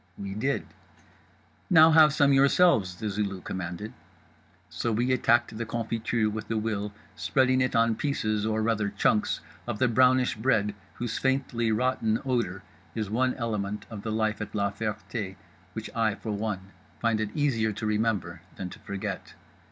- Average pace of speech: Yes, average, 160 wpm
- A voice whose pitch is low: Yes, low, 110 Hz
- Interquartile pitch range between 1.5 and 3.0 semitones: Yes, average, 2.7 semitones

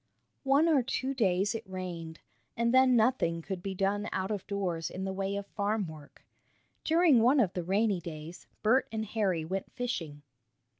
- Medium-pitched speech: No, high, 200 Hz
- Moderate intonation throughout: Yes, average, 4.6 semitones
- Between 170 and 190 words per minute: Yes, average, 180 wpm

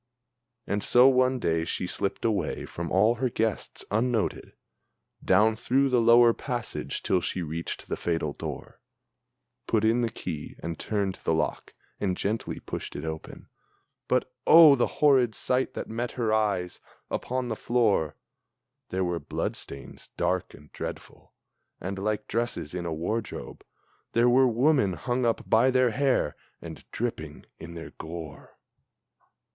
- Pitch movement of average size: No, wide, 6.0 semitones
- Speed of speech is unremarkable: Yes, average, 150 wpm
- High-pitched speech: No, low, 110 Hz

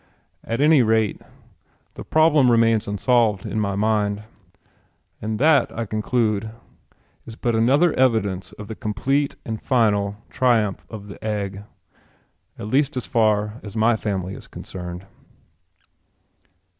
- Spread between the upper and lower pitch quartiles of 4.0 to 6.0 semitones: No, average, 3.0 semitones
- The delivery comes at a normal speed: No, slow, 130 wpm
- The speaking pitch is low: Yes, low, 110 Hz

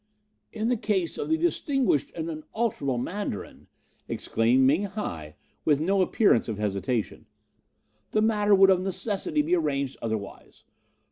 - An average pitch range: No, wide, 8.9 semitones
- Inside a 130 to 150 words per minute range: Yes, slow, 135 wpm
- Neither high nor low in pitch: Yes, medium, 180 Hz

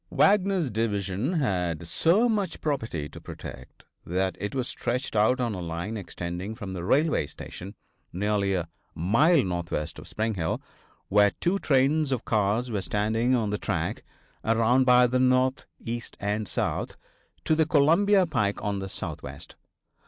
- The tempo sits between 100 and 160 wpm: Yes, average, 155 wpm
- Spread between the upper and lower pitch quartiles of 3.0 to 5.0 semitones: No, wide, 5.6 semitones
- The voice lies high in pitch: No, low, 110 Hz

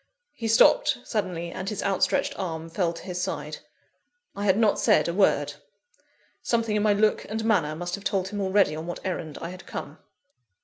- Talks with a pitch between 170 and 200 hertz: Yes, high, 190 Hz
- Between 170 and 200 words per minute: Yes, average, 190 wpm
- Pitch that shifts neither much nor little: Yes, average, 3.3 semitones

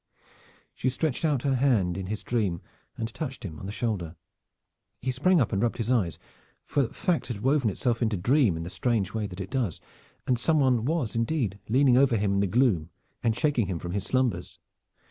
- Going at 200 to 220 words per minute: Yes, fast, 205 wpm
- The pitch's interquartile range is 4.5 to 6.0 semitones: Yes, average, 4.9 semitones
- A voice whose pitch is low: Yes, low, 115 Hz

